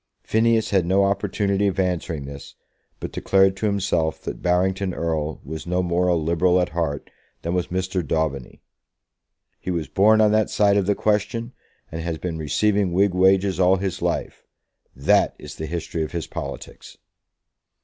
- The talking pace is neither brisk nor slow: Yes, average, 170 wpm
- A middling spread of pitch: Yes, average, 3.3 semitones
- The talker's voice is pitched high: No, very low, 90 Hz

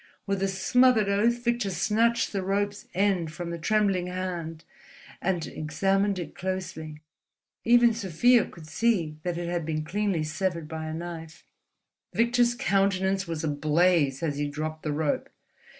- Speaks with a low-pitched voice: No, medium, 185 Hz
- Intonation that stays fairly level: No, average, 4.2 semitones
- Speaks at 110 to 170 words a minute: Yes, average, 150 wpm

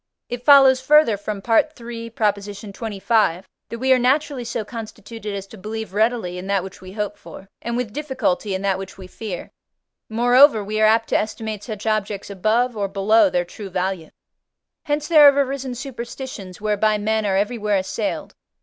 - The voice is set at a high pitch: Yes, high, 215 Hz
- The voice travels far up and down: No, average, 3.5 semitones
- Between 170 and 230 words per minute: Yes, average, 175 wpm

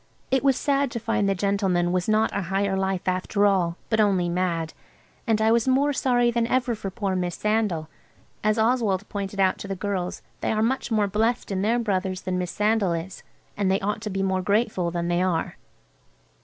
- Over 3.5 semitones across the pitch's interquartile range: No, average, 3.2 semitones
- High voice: Yes, high, 200 Hz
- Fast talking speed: Yes, fast, 210 wpm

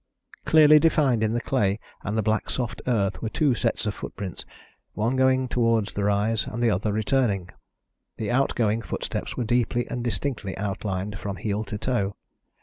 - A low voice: Yes, low, 110 Hz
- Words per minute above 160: Yes, average, 170 wpm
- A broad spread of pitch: No, average, 3.2 semitones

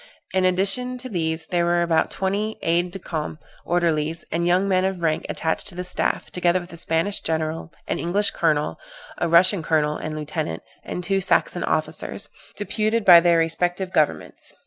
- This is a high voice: No, medium, 175 Hz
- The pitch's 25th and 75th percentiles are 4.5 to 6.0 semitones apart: No, average, 2.8 semitones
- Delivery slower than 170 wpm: No, average, 175 wpm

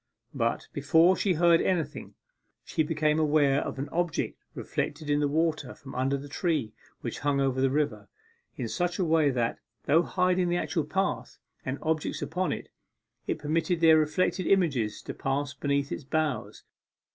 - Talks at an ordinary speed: Yes, average, 170 wpm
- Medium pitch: Yes, medium, 155 Hz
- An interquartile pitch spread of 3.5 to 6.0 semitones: No, average, 3.1 semitones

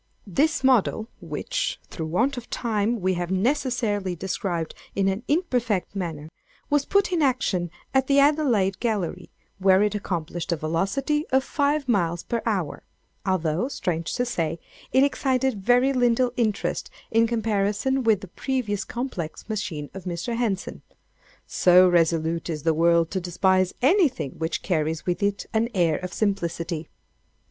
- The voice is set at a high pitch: Yes, high, 200 Hz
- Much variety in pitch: Yes, wide, 6.2 semitones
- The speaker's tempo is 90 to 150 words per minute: Yes, average, 145 wpm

